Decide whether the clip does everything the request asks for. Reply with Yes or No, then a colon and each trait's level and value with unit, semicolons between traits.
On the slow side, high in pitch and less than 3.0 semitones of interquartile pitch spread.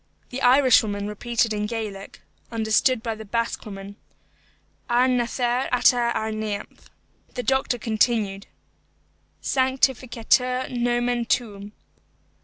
Yes: slow, 100 wpm; high, 235 Hz; narrow, 2.5 semitones